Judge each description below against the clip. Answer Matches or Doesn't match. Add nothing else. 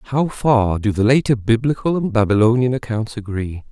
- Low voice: Matches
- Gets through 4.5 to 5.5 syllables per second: Matches